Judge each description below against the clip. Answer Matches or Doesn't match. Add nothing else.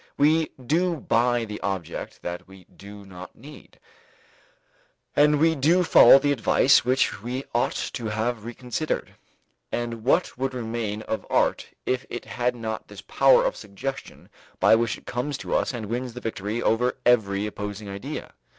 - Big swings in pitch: Doesn't match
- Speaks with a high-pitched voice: Doesn't match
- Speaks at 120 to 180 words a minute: Matches